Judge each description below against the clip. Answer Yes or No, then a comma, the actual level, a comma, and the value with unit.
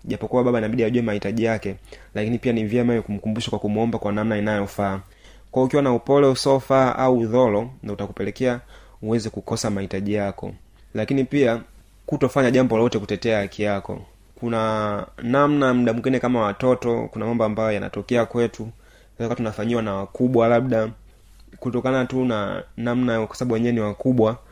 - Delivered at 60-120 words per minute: No, average, 130 wpm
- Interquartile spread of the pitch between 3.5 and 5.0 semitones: No, average, 3.0 semitones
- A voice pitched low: Yes, low, 115 Hz